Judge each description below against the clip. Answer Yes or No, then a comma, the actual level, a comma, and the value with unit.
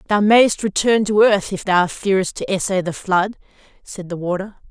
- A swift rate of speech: No, average, 190 wpm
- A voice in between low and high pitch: No, high, 195 Hz